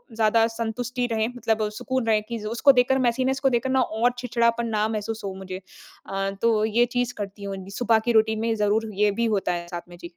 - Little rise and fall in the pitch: Yes, narrow, 2.3 semitones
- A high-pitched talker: Yes, high, 225 Hz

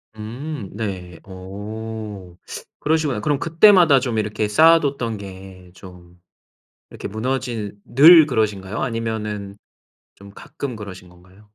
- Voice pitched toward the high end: No, low, 110 Hz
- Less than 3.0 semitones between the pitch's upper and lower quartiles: No, average, 5.3 semitones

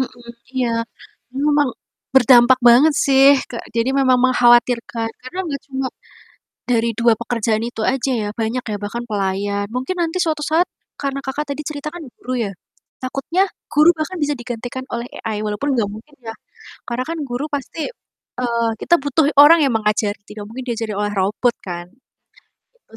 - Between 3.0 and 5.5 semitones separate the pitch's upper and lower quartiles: Yes, average, 3.8 semitones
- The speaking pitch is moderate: No, high, 245 Hz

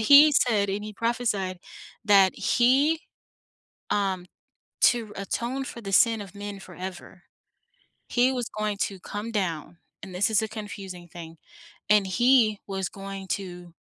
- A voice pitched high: Yes, high, 205 Hz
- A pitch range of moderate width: Yes, average, 3.4 semitones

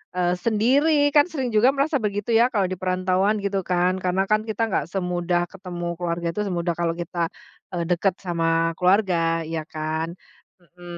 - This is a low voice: No, medium, 185 Hz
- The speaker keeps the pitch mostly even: No, average, 3.0 semitones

